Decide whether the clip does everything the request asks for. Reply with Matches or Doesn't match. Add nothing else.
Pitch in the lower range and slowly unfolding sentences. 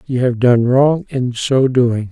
Doesn't match